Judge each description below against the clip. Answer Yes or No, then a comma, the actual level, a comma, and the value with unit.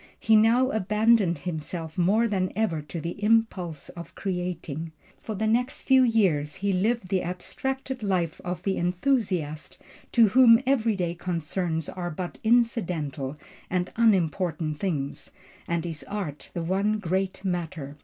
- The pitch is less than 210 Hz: Yes, medium, 185 Hz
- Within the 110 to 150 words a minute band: Yes, average, 145 wpm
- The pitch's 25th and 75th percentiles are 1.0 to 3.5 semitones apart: No, average, 4.7 semitones